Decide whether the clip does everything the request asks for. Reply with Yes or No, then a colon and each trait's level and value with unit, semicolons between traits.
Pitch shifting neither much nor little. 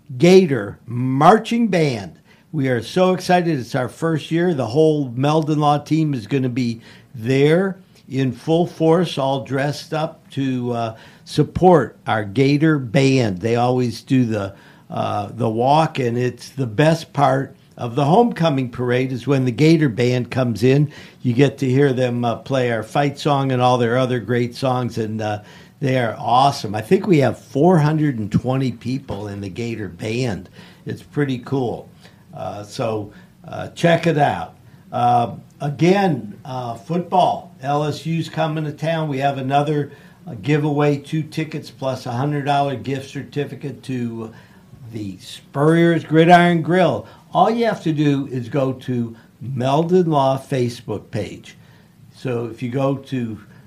Yes: average, 4.4 semitones